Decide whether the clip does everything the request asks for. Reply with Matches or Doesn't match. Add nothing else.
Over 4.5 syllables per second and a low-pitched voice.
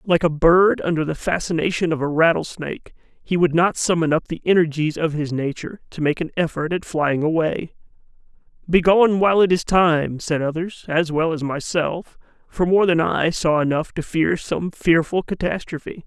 Doesn't match